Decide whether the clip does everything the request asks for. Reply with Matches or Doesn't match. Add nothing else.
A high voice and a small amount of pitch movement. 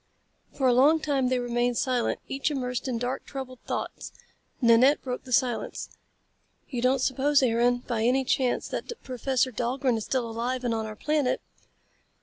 Matches